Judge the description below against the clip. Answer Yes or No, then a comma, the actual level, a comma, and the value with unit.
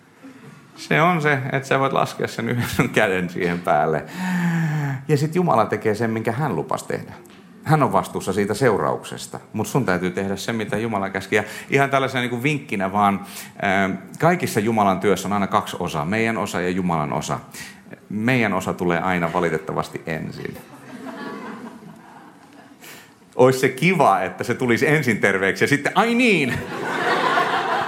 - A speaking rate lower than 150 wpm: No, fast, 155 wpm